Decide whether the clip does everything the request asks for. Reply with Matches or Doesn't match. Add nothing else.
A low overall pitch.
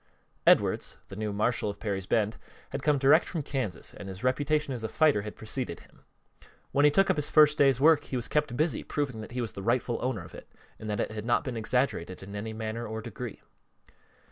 Matches